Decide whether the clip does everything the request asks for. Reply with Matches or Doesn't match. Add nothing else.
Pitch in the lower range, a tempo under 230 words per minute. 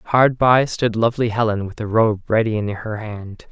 Matches